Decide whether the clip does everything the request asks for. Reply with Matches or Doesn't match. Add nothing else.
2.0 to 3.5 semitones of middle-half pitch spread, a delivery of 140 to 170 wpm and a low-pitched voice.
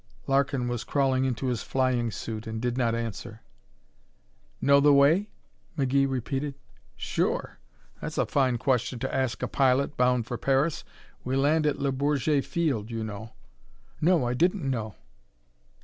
Matches